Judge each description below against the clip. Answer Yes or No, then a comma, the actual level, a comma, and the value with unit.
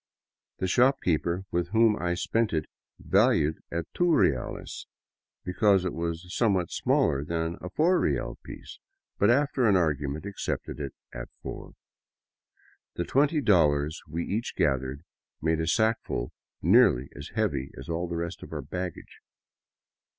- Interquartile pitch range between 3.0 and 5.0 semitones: No, wide, 5.4 semitones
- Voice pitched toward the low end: Yes, very low, 85 Hz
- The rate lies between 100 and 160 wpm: Yes, average, 145 wpm